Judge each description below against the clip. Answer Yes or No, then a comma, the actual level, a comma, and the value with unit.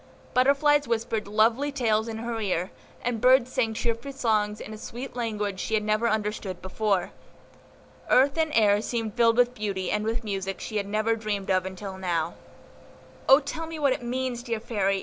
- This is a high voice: Yes, high, 220 Hz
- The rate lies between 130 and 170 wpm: No, average, 185 wpm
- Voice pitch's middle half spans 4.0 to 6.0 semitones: No, average, 3.0 semitones